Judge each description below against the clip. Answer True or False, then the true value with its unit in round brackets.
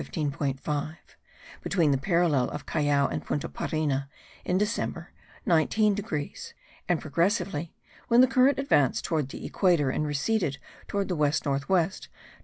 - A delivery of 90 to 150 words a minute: True (145 wpm)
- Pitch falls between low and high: True (155 Hz)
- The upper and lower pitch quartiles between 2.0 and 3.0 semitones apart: False (5.1 semitones)